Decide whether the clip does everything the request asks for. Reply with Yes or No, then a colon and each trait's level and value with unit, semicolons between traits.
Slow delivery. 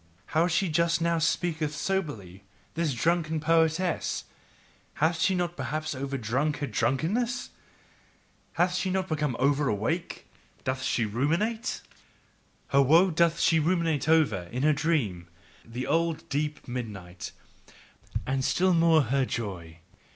Yes: slow, 120 wpm